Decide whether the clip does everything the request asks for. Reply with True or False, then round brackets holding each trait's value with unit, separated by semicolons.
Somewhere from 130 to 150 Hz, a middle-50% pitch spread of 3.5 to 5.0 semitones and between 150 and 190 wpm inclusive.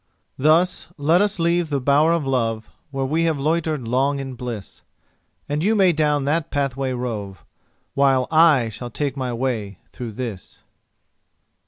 True (140 Hz; 4.1 semitones; 155 wpm)